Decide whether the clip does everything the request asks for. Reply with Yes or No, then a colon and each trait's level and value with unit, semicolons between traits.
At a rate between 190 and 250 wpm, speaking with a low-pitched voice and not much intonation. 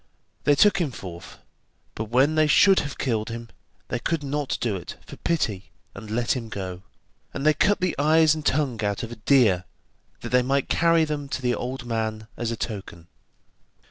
No: average, 195 wpm; low, 125 Hz; wide, 5.4 semitones